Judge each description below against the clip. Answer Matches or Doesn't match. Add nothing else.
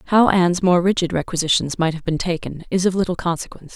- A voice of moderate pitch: Matches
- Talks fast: Matches